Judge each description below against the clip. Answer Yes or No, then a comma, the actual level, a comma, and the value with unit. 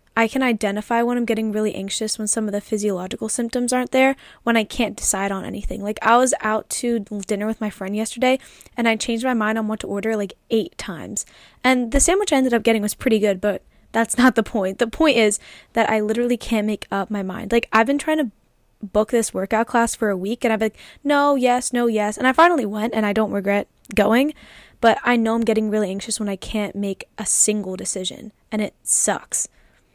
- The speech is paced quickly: Yes, fast, 230 wpm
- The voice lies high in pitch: Yes, high, 220 Hz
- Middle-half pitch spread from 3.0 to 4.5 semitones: No, narrow, 2.4 semitones